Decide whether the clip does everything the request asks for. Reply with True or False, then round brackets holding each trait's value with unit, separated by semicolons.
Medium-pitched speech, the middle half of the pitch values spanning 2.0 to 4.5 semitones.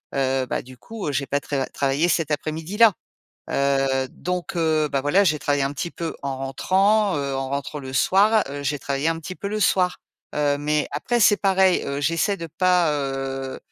False (150 Hz; 4.9 semitones)